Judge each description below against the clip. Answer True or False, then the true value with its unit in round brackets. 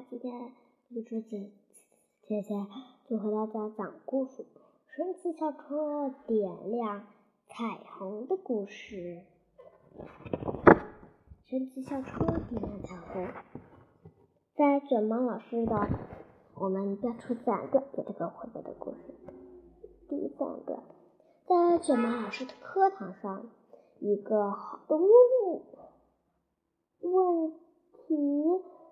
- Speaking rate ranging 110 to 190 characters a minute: True (160 characters per minute)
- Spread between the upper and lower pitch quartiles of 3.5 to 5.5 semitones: False (6.6 semitones)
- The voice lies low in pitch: False (245 Hz)